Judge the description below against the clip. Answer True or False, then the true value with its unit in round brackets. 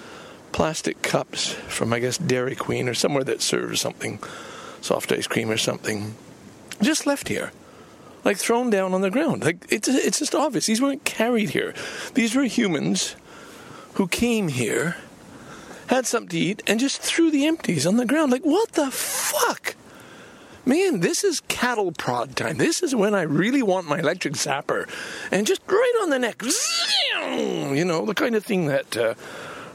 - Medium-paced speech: True (175 wpm)